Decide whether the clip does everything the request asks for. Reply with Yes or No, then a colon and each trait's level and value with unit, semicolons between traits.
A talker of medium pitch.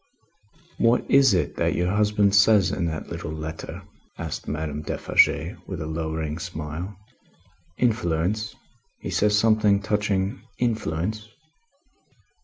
No: very low, 95 Hz